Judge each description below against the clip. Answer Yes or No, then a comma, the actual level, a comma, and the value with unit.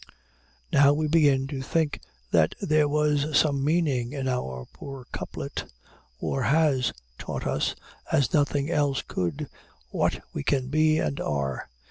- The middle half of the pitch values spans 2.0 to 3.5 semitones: Yes, average, 2.9 semitones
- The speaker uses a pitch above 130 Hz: Yes, medium, 140 Hz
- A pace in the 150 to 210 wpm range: No, average, 140 wpm